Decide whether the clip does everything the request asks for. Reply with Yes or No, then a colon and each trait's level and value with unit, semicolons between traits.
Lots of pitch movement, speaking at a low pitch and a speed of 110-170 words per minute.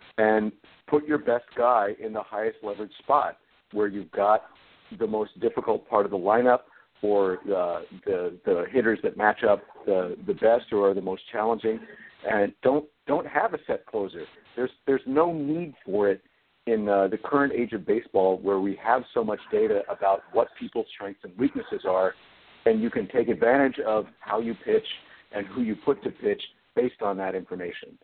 No: wide, 6.9 semitones; low, 115 Hz; average, 190 wpm